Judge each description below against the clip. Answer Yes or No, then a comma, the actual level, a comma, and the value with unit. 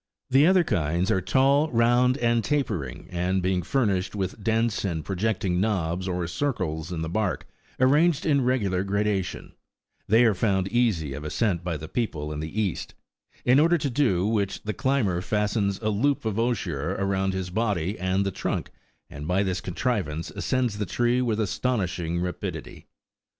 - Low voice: Yes, low, 100 Hz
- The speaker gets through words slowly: No, average, 170 wpm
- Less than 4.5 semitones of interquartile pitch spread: No, average, 5.0 semitones